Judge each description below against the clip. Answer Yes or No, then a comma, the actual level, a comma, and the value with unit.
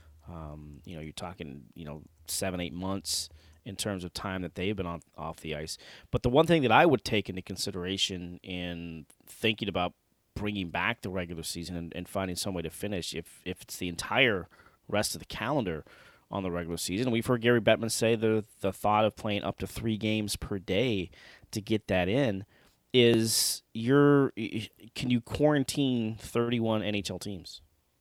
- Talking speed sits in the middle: Yes, average, 190 wpm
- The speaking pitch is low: Yes, very low, 95 Hz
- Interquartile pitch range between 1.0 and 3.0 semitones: No, average, 4.3 semitones